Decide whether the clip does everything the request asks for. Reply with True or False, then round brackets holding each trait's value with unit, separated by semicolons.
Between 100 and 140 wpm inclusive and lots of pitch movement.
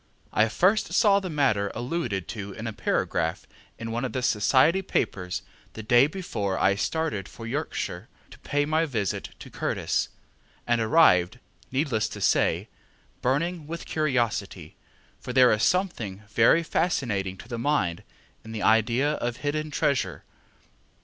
False (150 wpm; 6.3 semitones)